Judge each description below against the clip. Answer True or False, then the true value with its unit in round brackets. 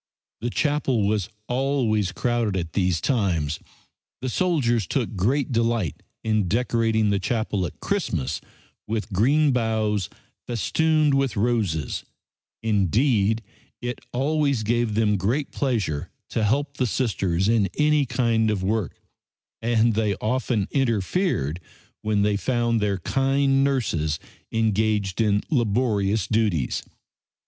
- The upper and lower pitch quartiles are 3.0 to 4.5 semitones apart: True (4.1 semitones)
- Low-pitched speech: True (110 Hz)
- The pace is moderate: False (120 wpm)